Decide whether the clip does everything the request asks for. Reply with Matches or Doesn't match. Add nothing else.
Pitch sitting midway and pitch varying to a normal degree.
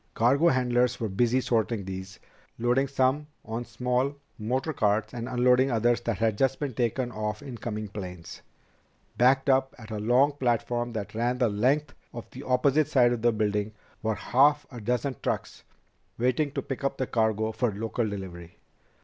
Doesn't match